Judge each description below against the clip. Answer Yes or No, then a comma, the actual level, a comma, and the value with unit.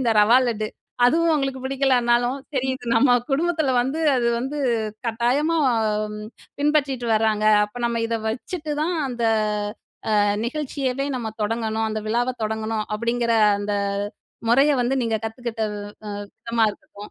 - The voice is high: Yes, high, 245 Hz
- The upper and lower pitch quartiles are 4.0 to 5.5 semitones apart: No, average, 3.3 semitones